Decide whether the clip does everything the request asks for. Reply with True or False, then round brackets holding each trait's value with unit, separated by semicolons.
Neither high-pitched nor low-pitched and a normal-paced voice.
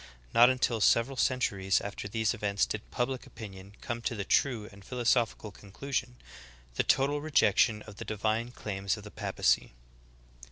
False (110 Hz; 170 wpm)